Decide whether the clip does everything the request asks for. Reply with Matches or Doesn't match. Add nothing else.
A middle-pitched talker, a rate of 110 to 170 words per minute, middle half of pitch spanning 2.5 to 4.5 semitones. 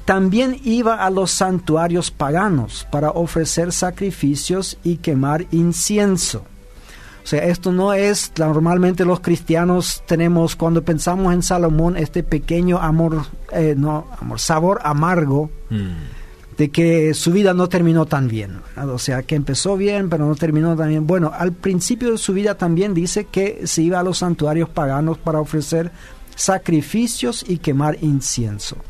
Matches